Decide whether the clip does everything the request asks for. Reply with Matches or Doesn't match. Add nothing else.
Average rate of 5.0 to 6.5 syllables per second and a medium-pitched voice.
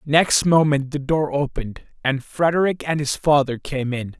Doesn't match